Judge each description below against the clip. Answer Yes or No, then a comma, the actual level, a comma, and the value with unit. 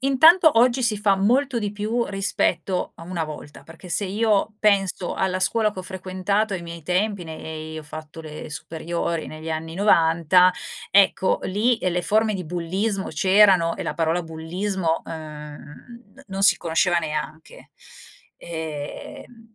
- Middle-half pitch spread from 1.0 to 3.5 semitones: No, average, 4.3 semitones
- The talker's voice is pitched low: No, medium, 185 Hz